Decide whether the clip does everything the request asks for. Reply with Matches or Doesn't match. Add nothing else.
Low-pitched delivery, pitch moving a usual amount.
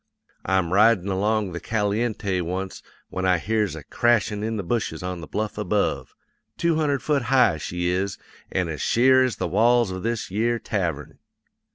Matches